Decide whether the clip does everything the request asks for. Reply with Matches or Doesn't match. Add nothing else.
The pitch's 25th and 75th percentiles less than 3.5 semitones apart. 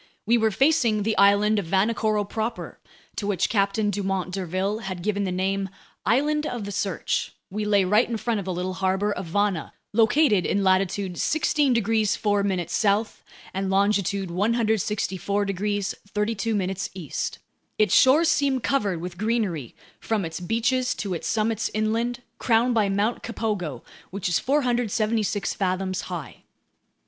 Matches